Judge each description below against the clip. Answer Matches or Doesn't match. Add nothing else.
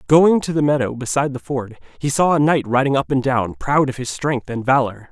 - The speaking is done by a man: Matches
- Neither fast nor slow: Doesn't match